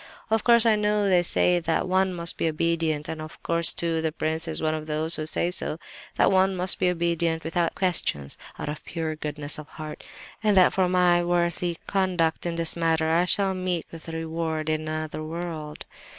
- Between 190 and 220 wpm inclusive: Yes, average, 200 wpm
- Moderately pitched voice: Yes, medium, 165 Hz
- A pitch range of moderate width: No, narrow, 2.3 semitones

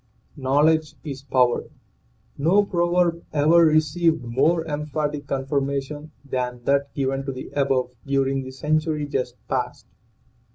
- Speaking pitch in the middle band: Yes, medium, 145 Hz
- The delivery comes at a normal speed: No, slow, 125 wpm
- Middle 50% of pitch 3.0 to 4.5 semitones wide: No, narrow, 2.6 semitones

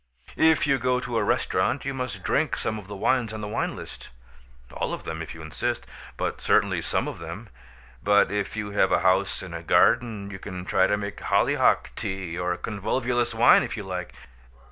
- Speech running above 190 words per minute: Yes, average, 200 wpm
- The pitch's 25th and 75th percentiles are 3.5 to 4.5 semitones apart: Yes, average, 4.1 semitones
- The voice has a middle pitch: No, low, 100 Hz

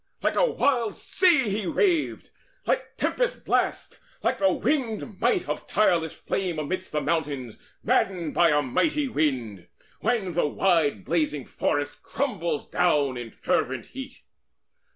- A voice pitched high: No, medium, 175 Hz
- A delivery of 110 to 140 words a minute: Yes, slow, 135 wpm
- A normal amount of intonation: No, wide, 8.9 semitones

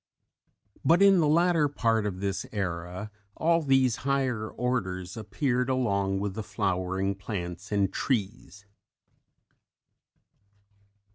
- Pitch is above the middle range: No, low, 105 Hz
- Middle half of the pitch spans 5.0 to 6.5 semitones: Yes, wide, 5.5 semitones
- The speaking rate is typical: No, slow, 110 wpm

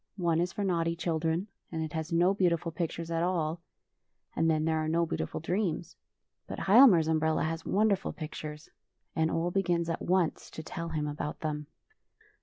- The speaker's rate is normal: Yes, average, 180 wpm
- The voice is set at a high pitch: No, medium, 165 Hz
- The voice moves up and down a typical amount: No, narrow, 1.7 semitones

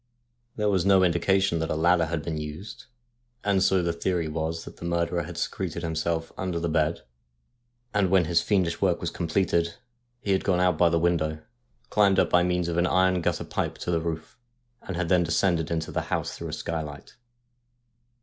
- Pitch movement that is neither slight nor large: No, narrow, 2.1 semitones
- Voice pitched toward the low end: Yes, very low, 85 Hz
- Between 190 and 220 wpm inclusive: Yes, average, 195 wpm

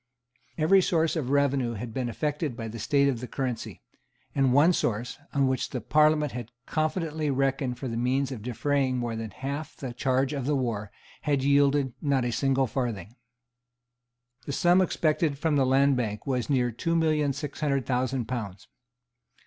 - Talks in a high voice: No, low, 135 Hz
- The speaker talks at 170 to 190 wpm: Yes, average, 175 wpm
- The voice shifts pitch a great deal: No, average, 3.0 semitones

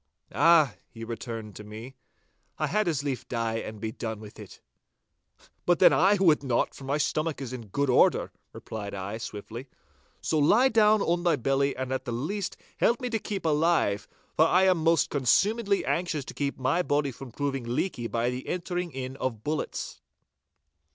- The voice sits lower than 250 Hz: Yes, medium, 140 Hz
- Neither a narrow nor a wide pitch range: No, wide, 6.5 semitones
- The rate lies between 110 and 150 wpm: No, average, 185 wpm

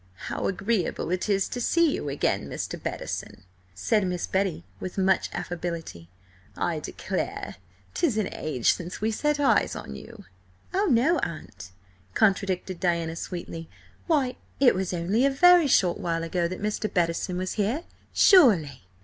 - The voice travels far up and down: Yes, wide, 6.2 semitones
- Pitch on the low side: No, medium, 185 Hz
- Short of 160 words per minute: Yes, average, 150 wpm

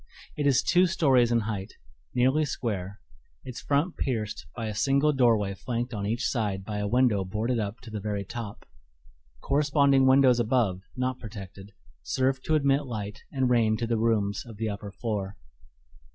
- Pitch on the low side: Yes, low, 115 Hz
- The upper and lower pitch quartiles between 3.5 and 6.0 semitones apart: Yes, average, 4.2 semitones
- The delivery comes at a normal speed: Yes, average, 170 wpm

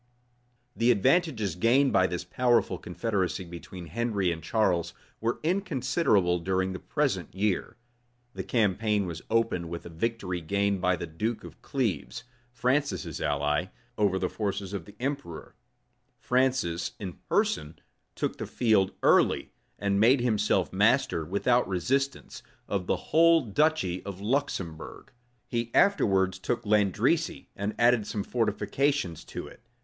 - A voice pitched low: Yes, low, 100 Hz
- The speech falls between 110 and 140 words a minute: Yes, slow, 135 wpm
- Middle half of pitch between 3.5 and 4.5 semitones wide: No, average, 5.1 semitones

